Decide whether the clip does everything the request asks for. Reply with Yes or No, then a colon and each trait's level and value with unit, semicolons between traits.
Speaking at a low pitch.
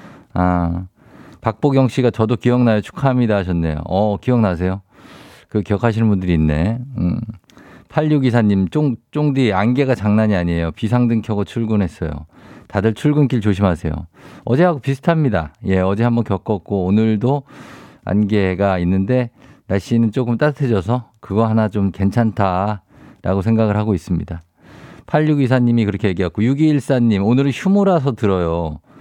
Yes: low, 110 Hz